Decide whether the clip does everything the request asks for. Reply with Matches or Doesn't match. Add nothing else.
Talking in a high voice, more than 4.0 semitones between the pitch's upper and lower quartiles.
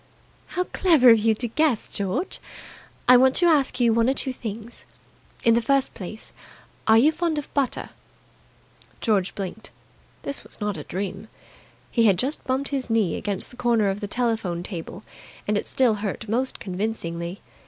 Matches